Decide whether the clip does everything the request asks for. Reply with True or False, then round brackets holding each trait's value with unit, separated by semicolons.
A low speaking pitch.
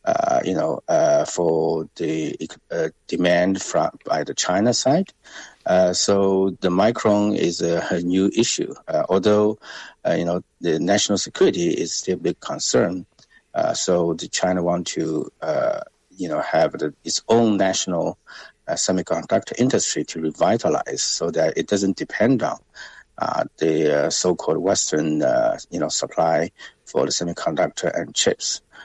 True (100 Hz)